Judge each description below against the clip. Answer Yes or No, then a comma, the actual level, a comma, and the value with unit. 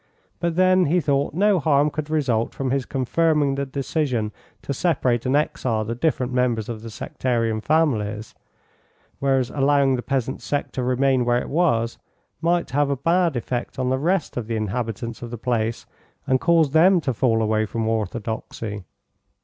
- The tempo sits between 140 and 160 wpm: No, average, 175 wpm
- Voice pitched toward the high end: No, low, 130 Hz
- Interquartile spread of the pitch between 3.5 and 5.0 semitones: Yes, average, 4.3 semitones